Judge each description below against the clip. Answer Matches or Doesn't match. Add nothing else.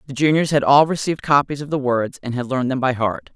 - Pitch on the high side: Doesn't match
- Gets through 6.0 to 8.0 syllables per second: Matches